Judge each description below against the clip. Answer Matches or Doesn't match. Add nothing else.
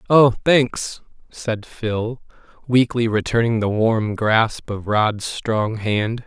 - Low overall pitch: Matches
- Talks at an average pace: Doesn't match